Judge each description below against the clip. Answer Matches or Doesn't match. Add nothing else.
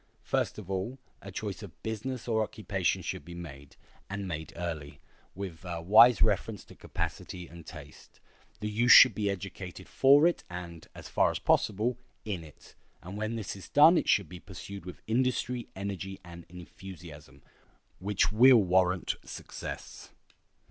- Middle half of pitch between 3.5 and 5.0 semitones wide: Matches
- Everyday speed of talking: Matches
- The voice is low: Matches